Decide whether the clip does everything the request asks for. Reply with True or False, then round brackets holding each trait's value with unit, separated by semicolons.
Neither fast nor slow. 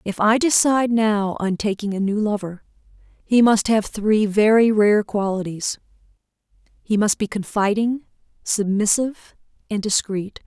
False (130 wpm)